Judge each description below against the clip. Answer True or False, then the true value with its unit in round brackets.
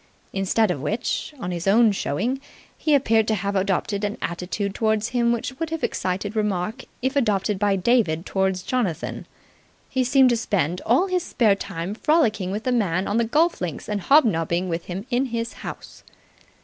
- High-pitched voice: True (210 Hz)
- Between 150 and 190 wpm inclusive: True (180 wpm)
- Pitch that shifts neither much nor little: True (4.5 semitones)